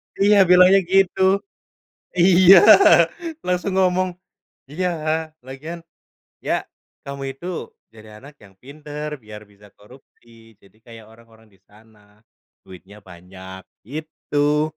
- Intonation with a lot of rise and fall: Yes, wide, 8.4 semitones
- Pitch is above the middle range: No, low, 135 Hz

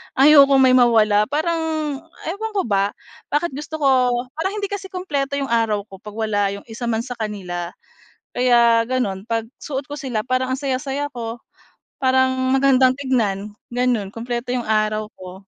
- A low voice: No, high, 245 Hz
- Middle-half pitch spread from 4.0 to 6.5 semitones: Yes, average, 4.3 semitones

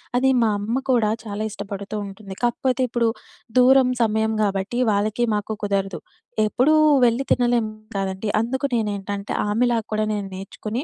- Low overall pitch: No, high, 215 Hz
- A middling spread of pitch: Yes, average, 3.1 semitones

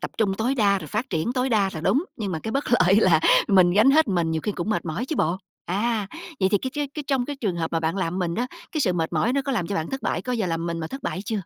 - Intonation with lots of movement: Yes, wide, 6.4 semitones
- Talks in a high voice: Yes, high, 200 Hz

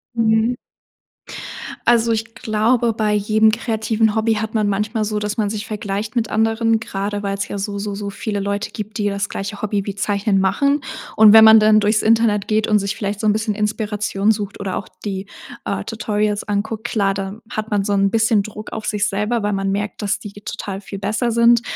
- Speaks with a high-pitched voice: Yes, high, 210 Hz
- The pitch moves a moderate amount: No, narrow, 1.5 semitones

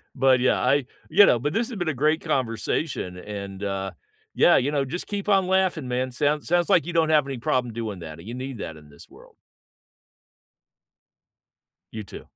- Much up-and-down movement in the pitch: Yes, wide, 6.4 semitones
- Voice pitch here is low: Yes, low, 130 Hz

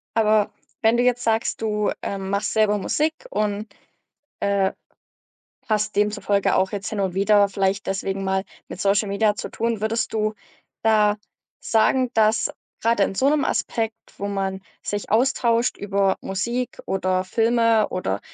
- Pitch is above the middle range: Yes, high, 210 Hz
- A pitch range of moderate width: No, narrow, 2.2 semitones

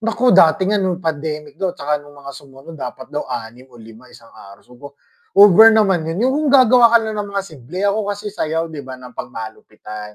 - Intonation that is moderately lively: No, wide, 7.8 semitones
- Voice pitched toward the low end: No, medium, 160 Hz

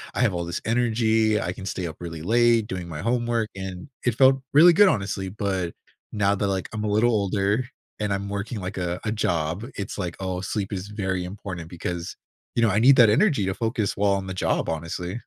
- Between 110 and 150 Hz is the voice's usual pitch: No, low, 100 Hz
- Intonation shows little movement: No, average, 3.6 semitones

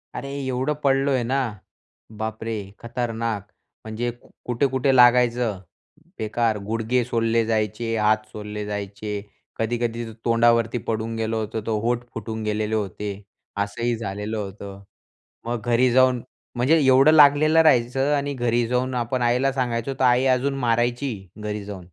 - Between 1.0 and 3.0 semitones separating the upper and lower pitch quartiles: Yes, narrow, 2.5 semitones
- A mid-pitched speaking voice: No, low, 115 Hz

